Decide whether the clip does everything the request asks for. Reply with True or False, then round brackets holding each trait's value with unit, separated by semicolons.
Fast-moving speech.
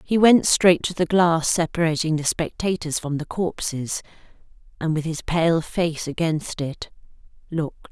False (150 wpm)